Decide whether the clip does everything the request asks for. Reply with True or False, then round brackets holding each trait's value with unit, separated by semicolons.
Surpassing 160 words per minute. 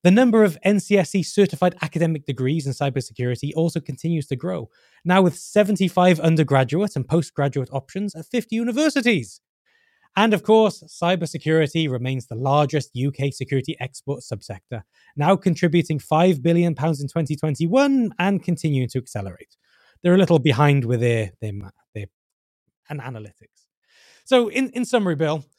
False (140 wpm)